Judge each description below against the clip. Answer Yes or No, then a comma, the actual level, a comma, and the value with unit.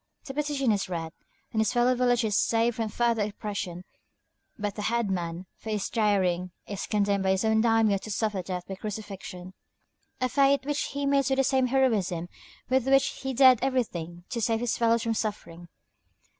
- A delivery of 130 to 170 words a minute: No, average, 185 wpm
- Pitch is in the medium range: No, high, 220 Hz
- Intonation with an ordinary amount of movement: Yes, average, 4.6 semitones